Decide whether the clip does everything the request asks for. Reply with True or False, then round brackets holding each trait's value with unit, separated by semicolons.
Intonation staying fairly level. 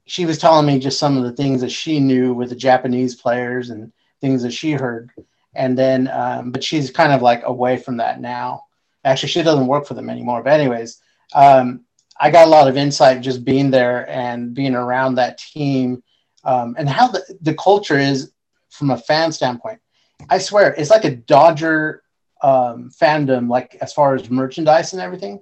False (3.6 semitones)